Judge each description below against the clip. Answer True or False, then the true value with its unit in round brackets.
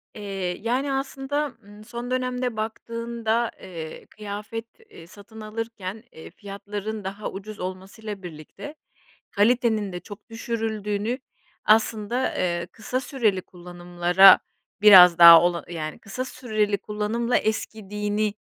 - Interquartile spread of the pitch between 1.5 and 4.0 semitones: True (3.4 semitones)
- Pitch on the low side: False (210 Hz)